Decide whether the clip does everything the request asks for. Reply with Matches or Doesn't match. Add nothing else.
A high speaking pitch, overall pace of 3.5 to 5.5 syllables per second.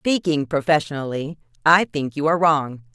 Doesn't match